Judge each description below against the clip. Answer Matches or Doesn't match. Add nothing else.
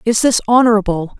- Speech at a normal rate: Matches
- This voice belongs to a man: Doesn't match